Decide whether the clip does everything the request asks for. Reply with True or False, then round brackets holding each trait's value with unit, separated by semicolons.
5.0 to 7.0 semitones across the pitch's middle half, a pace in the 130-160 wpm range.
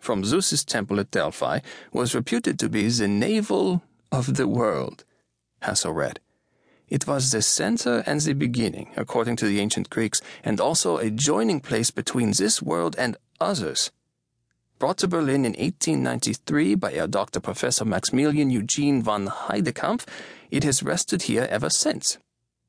True (5.6 semitones; 155 wpm)